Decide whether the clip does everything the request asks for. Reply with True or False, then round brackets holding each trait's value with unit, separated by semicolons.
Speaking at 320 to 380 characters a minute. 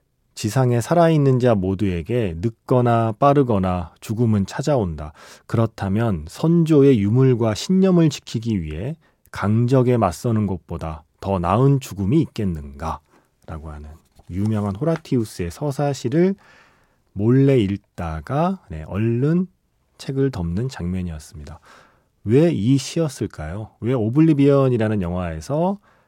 False (270 characters per minute)